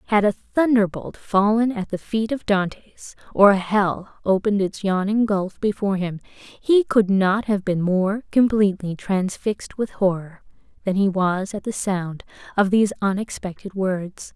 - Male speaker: No, female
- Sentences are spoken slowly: No, average, 155 wpm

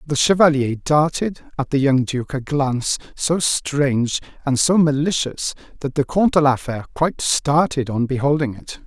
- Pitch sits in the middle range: Yes, medium, 145 Hz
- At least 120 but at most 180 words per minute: Yes, average, 170 wpm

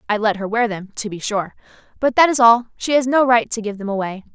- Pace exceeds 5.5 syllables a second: Yes, 6.0 syllables/s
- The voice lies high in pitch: Yes, high, 225 Hz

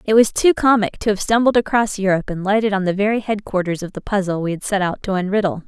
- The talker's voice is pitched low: No, high, 200 Hz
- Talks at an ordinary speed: No, fast, 255 wpm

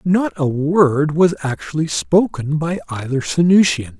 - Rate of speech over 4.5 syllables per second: No, 4.0 syllables/s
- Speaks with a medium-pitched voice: Yes, medium, 160 Hz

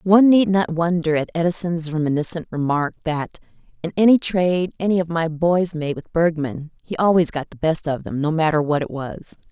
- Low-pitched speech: No, medium, 165 Hz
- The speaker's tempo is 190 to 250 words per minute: Yes, average, 195 wpm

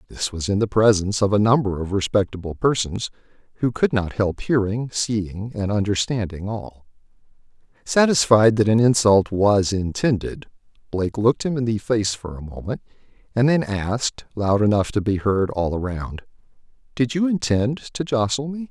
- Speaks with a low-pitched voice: Yes, low, 110 Hz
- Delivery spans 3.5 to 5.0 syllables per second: Yes, 4.9 syllables/s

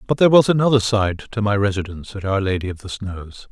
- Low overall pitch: Yes, low, 105 Hz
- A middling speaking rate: No, fast, 240 wpm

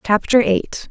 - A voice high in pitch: Yes, high, 215 Hz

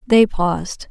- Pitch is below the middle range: No, high, 195 Hz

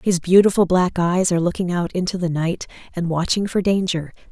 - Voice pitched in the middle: Yes, medium, 180 Hz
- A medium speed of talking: Yes, average, 195 wpm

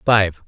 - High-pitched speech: No, very low, 95 Hz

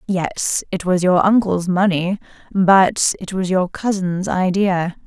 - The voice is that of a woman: Yes, female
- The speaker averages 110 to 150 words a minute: Yes, average, 140 wpm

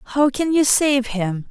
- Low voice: No, very high, 260 Hz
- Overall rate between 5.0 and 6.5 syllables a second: No, 3.5 syllables/s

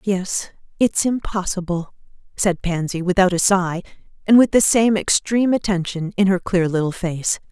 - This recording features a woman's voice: Yes, female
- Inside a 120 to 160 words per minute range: Yes, average, 150 wpm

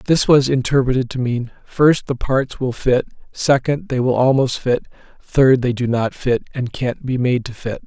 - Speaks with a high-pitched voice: No, low, 130 Hz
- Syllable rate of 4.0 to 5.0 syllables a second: Yes, 4.5 syllables/s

